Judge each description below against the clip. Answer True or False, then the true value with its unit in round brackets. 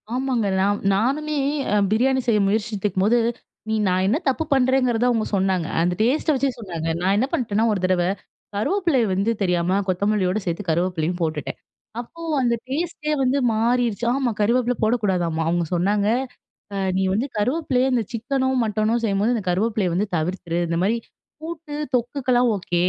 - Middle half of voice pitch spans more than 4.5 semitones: True (5.1 semitones)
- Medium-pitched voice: False (215 Hz)